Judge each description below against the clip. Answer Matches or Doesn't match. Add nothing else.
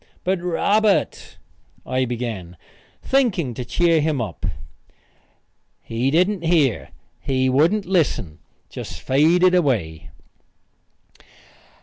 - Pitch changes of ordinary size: Doesn't match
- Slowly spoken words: Matches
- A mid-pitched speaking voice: Matches